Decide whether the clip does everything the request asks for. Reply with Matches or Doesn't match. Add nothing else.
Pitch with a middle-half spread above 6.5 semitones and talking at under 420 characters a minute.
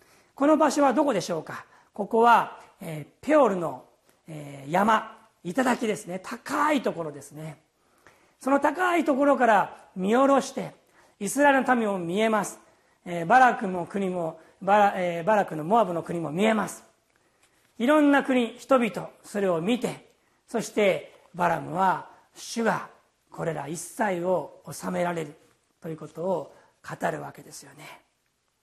Matches